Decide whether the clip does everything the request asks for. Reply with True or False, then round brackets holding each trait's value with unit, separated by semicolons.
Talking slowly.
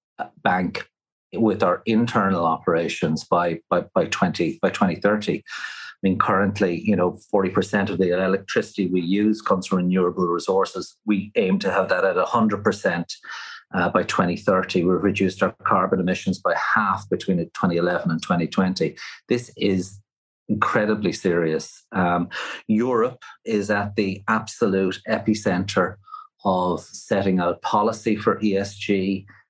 True (130 wpm)